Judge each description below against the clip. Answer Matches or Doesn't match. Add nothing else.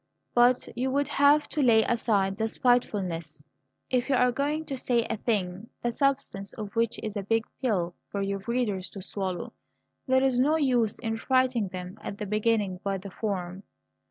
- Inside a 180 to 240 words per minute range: Matches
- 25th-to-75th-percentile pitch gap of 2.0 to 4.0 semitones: Doesn't match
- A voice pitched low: Doesn't match